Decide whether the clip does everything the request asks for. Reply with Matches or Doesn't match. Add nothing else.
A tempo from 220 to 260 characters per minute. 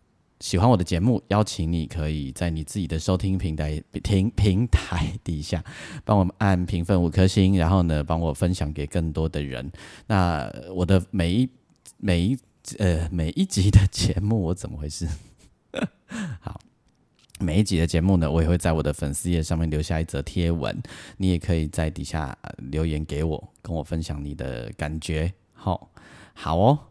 Matches